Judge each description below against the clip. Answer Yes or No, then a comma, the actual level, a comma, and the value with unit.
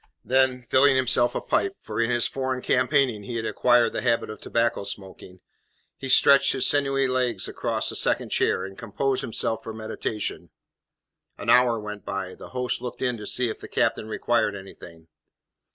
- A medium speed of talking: Yes, average, 180 wpm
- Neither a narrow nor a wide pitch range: Yes, average, 3.2 semitones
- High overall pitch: No, low, 120 Hz